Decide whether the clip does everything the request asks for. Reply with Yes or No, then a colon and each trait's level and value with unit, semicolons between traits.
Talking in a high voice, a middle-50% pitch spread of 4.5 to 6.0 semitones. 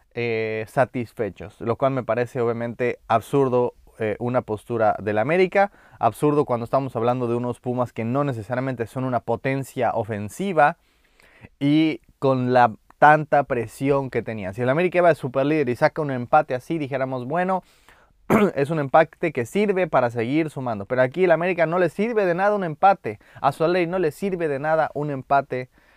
No: low, 135 Hz; average, 4.9 semitones